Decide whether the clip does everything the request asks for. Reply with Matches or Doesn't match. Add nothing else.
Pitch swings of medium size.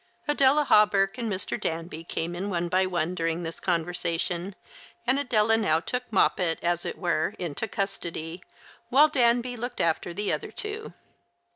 Doesn't match